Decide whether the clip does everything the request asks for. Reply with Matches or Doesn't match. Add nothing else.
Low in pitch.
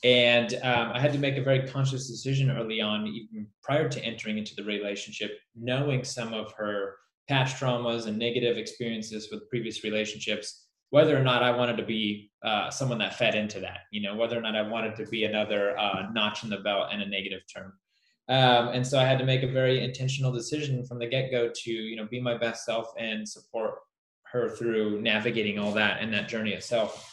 Matches